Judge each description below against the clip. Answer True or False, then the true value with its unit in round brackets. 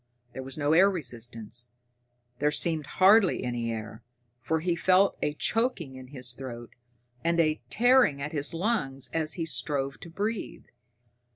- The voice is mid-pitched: True (150 Hz)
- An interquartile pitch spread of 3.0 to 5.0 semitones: False (5.5 semitones)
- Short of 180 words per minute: True (155 wpm)